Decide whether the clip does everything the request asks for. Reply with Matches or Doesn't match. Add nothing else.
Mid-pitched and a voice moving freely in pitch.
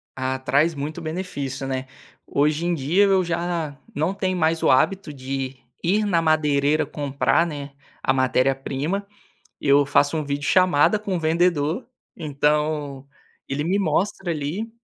Doesn't match